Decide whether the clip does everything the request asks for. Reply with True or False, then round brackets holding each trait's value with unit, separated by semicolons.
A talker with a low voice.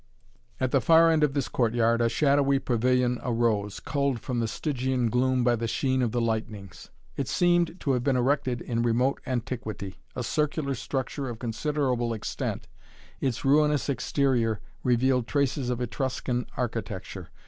True (125 Hz)